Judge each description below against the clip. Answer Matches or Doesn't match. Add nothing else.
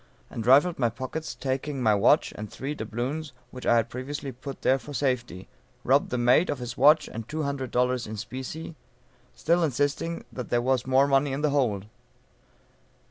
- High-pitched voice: Doesn't match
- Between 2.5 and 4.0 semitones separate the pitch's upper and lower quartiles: Matches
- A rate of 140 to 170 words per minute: Doesn't match